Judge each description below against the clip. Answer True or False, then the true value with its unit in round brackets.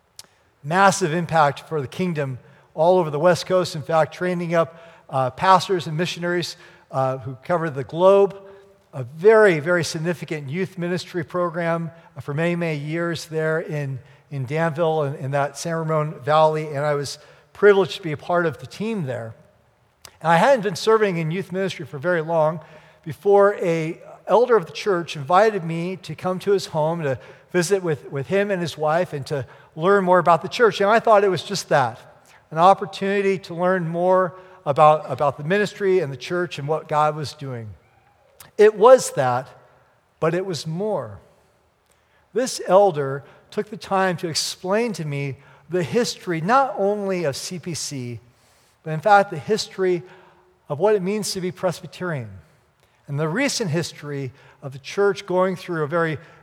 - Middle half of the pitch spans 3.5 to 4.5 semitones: True (4.2 semitones)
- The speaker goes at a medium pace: True (175 wpm)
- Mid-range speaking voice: True (170 Hz)